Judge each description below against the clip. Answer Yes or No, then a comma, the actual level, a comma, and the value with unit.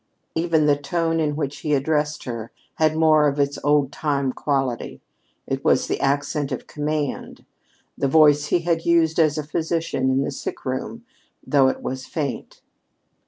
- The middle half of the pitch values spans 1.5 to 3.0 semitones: Yes, narrow, 2.4 semitones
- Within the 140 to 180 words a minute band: Yes, average, 165 wpm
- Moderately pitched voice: Yes, medium, 150 Hz